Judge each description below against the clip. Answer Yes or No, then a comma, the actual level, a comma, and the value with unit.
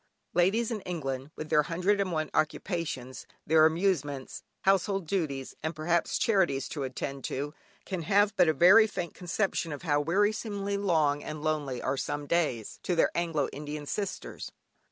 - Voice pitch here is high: No, medium, 165 Hz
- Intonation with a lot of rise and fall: No, average, 4.8 semitones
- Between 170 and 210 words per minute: No, average, 160 wpm